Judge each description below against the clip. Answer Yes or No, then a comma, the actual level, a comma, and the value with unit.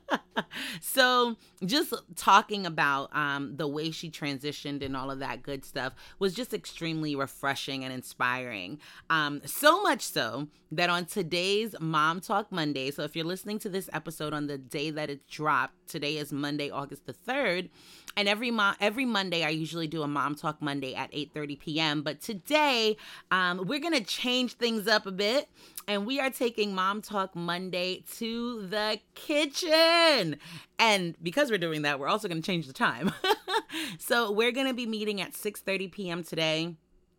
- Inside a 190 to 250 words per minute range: No, average, 175 wpm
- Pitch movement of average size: No, wide, 6.4 semitones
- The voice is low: No, medium, 180 Hz